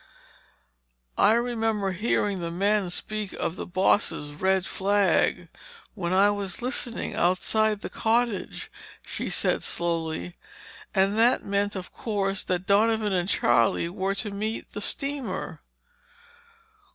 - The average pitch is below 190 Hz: No, high, 200 Hz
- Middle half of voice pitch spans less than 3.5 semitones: Yes, average, 2.8 semitones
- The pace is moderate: No, slow, 125 wpm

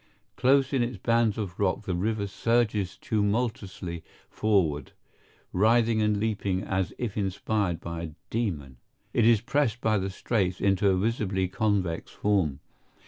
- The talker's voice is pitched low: Yes, low, 105 Hz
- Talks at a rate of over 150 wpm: No, average, 140 wpm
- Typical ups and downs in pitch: Yes, average, 3.3 semitones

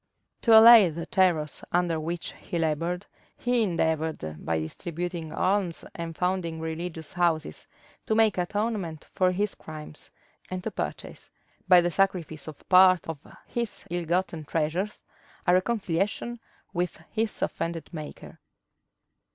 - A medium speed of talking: No, slow, 130 wpm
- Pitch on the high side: No, medium, 175 Hz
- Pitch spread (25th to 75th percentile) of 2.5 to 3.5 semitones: Yes, average, 2.8 semitones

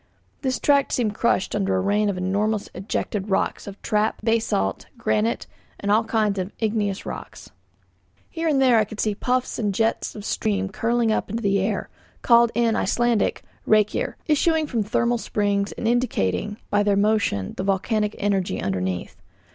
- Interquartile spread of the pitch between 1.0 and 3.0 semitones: Yes, average, 2.7 semitones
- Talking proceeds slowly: No, average, 165 wpm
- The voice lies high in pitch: Yes, high, 210 Hz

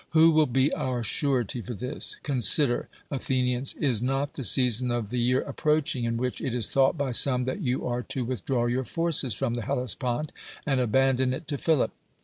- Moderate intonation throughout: No, narrow, 2.3 semitones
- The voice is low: Yes, low, 130 Hz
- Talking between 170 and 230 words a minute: Yes, average, 195 wpm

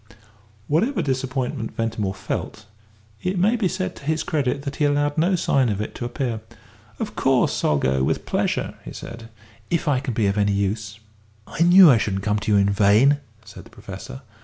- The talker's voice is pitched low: Yes, low, 125 Hz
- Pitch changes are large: Yes, wide, 6.9 semitones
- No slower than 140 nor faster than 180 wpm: No, average, 195 wpm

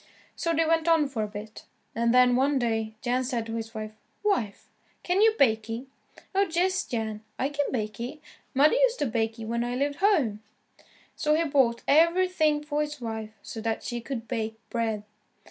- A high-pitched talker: Yes, very high, 250 Hz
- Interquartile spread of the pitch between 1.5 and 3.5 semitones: No, wide, 5.4 semitones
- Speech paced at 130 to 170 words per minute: No, average, 195 wpm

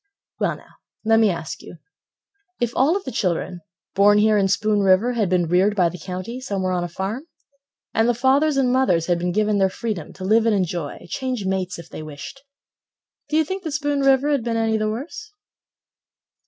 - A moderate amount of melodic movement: No, wide, 5.8 semitones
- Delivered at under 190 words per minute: No, fast, 205 wpm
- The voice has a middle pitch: No, high, 215 Hz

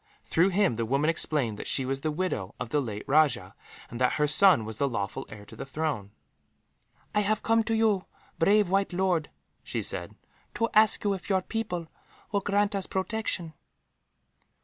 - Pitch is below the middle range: No, medium, 170 Hz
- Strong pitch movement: Yes, wide, 6.8 semitones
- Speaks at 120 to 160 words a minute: No, average, 185 wpm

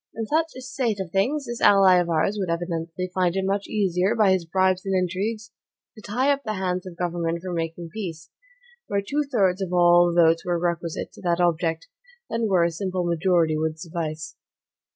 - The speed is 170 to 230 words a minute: Yes, average, 200 wpm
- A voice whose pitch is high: No, medium, 180 Hz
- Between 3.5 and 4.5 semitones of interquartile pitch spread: No, average, 2.9 semitones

